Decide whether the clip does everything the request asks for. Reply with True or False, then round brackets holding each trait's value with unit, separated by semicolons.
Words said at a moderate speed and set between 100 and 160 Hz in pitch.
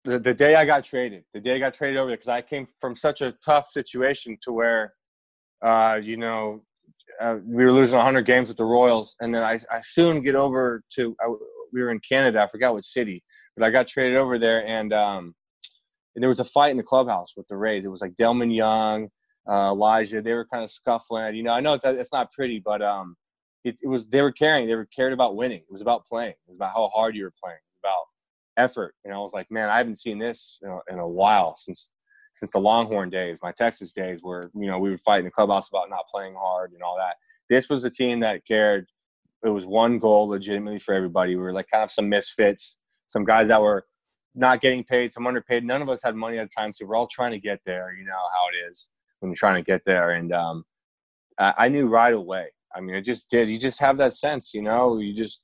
False (250 wpm; 115 Hz)